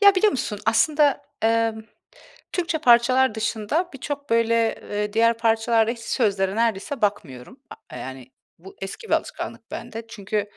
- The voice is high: Yes, high, 230 Hz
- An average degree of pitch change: Yes, average, 3.9 semitones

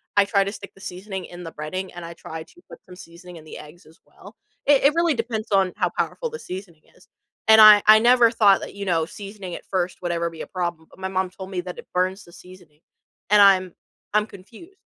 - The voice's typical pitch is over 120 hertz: Yes, high, 190 Hz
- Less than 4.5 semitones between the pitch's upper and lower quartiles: Yes, average, 3.2 semitones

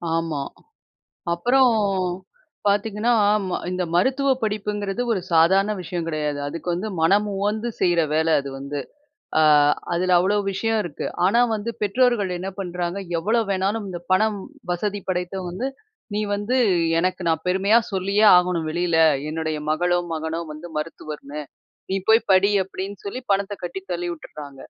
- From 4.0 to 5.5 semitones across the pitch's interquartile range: No, average, 3.6 semitones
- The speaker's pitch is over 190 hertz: No, medium, 185 Hz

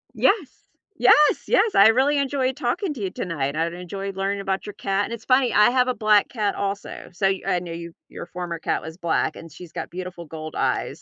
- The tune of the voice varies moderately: No, wide, 6.2 semitones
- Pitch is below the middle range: No, high, 195 Hz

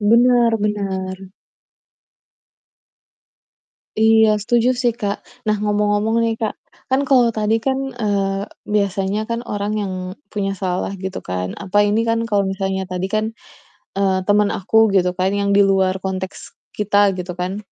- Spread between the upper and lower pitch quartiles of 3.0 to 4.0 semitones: No, narrow, 2.6 semitones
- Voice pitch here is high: Yes, high, 205 Hz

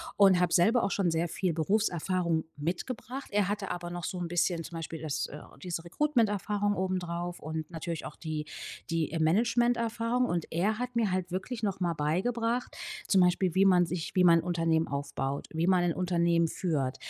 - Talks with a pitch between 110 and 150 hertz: No, medium, 175 Hz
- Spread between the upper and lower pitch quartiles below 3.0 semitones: No, average, 3.7 semitones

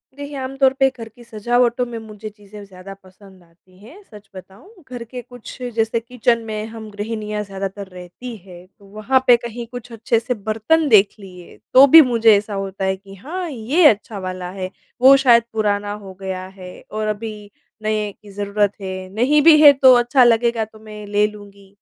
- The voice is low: No, high, 215 Hz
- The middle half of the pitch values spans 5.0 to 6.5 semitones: No, average, 3.6 semitones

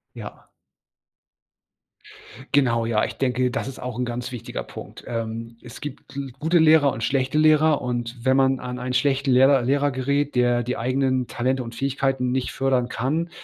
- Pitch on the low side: Yes, low, 130 Hz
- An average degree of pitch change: No, narrow, 2.1 semitones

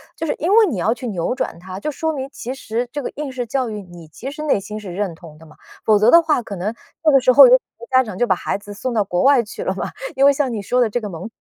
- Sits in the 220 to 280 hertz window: Yes, high, 235 Hz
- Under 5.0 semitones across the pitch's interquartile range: No, wide, 5.5 semitones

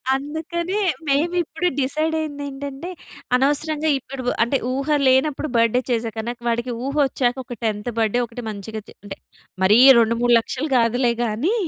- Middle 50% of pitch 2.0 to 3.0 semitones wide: No, average, 4.6 semitones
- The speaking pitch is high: Yes, very high, 265 Hz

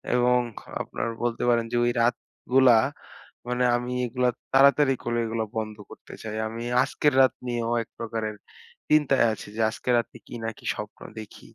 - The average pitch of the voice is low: Yes, low, 120 Hz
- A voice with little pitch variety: Yes, narrow, 2.0 semitones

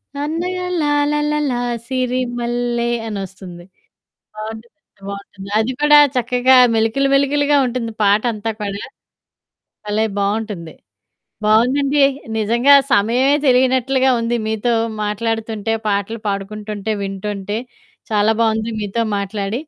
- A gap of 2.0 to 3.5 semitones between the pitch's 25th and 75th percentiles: No, average, 4.0 semitones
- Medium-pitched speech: No, high, 225 Hz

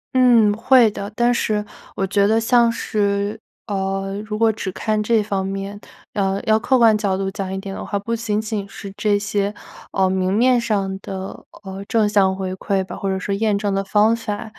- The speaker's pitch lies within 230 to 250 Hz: No, high, 205 Hz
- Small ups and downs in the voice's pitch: Yes, narrow, 2.1 semitones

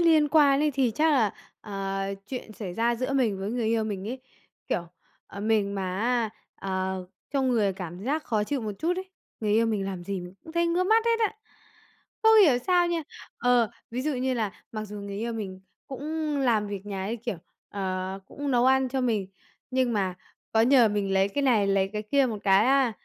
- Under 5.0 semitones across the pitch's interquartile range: No, average, 5.3 semitones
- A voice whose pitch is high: Yes, high, 230 Hz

